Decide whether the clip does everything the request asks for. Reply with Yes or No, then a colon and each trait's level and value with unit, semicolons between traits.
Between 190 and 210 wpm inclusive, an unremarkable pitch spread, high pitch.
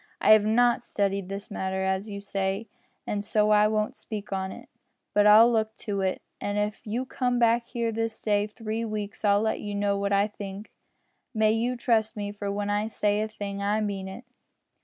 No: fast, 205 wpm; narrow, 1.6 semitones; high, 210 Hz